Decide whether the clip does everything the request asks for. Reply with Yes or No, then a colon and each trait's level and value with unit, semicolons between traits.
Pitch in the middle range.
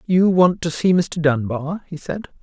Yes: medium, 165 Hz